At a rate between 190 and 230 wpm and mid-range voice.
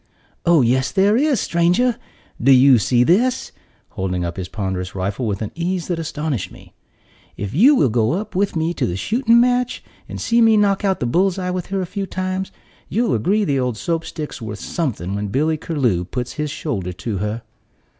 Yes: average, 195 wpm; medium, 155 Hz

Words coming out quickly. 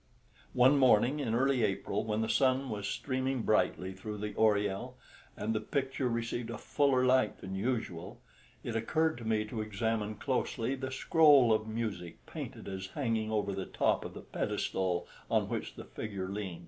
No: average, 175 wpm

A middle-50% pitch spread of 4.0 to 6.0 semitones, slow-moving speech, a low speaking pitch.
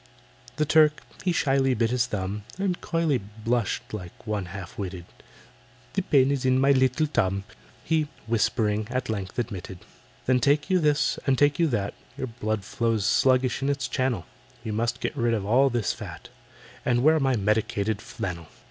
No: average, 4.7 semitones; average, 175 wpm; low, 120 Hz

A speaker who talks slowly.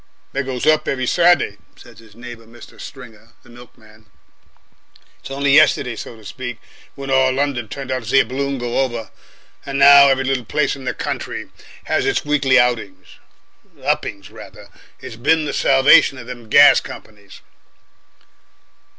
No: average, 160 wpm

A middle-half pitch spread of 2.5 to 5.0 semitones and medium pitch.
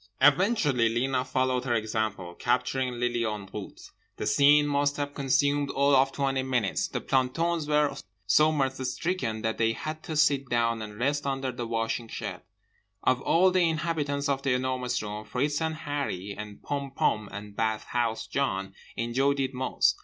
No: average, 3.7 semitones; low, 130 Hz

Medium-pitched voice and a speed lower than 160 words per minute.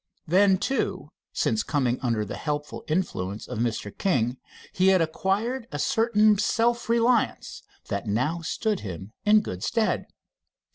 Yes: medium, 180 Hz; average, 140 wpm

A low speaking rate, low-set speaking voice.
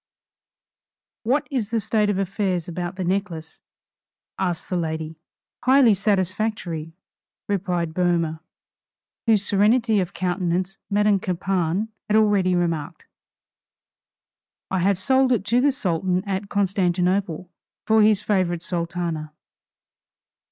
No: slow, 110 wpm; high, 190 Hz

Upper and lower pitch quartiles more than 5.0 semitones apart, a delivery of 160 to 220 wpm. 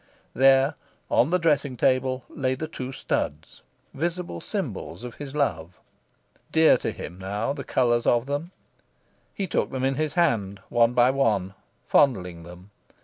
No: wide, 5.5 semitones; average, 150 wpm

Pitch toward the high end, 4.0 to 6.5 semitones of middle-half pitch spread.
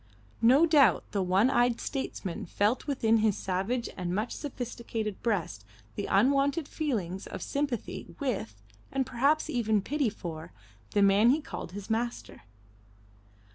Yes: high, 230 Hz; wide, 5.4 semitones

